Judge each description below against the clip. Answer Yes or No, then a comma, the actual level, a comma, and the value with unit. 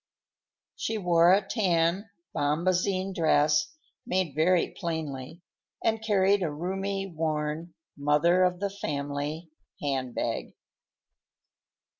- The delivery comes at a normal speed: No, slow, 95 wpm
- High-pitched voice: No, medium, 170 Hz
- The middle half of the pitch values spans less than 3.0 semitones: No, average, 4.0 semitones